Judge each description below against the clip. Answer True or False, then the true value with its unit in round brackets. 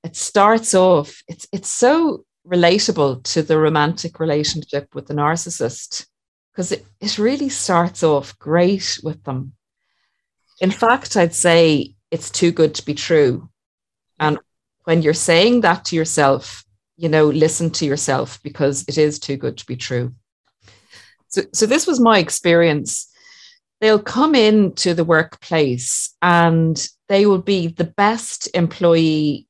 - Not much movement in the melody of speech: False (4.4 semitones)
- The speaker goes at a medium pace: True (145 wpm)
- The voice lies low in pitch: False (165 Hz)